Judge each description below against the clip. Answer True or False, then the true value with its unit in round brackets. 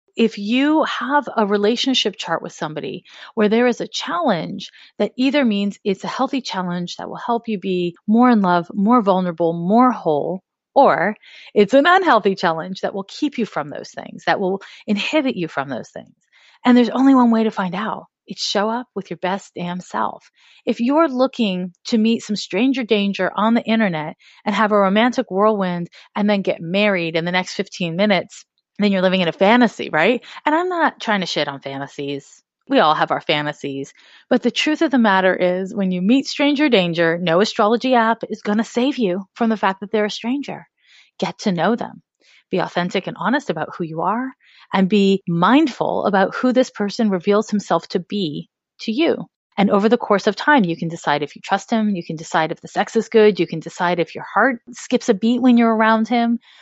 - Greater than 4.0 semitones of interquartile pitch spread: True (4.6 semitones)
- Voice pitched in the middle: False (210 Hz)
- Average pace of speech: False (210 wpm)